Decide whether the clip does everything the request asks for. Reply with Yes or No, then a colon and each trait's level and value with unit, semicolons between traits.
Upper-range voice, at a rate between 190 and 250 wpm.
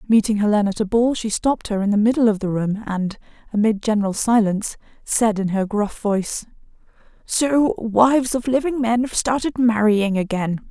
No: high, 220 Hz; average, 180 wpm